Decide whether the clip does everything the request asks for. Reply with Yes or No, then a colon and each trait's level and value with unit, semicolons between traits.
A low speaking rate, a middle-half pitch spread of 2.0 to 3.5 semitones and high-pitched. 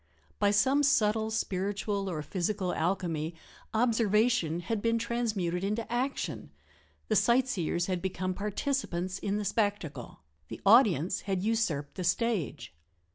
No: slow, 125 wpm; average, 4.2 semitones; high, 200 Hz